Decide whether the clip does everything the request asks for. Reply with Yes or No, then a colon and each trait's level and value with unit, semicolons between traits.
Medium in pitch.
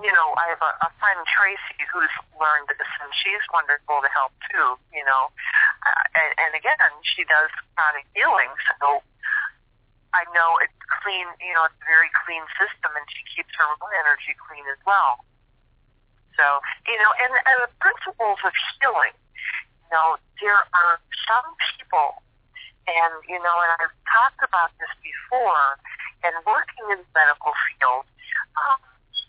Yes: medium, 170 Hz